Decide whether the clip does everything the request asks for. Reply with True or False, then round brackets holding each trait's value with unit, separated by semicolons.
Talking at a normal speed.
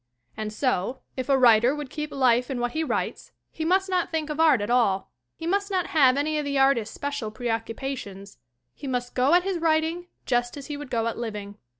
False (220 wpm)